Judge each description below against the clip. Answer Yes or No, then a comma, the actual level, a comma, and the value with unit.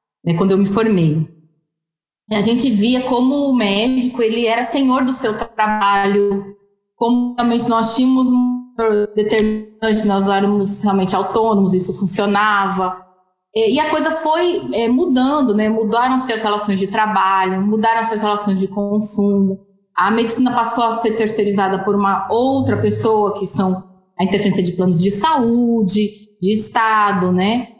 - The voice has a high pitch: Yes, high, 210 Hz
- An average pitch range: Yes, average, 3.0 semitones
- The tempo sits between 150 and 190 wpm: No, average, 140 wpm